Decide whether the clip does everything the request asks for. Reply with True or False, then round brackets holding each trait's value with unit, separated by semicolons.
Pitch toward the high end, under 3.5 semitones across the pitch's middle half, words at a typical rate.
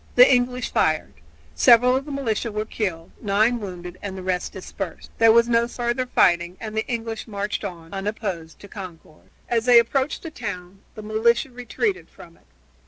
False (220 Hz; 4.2 semitones; 175 wpm)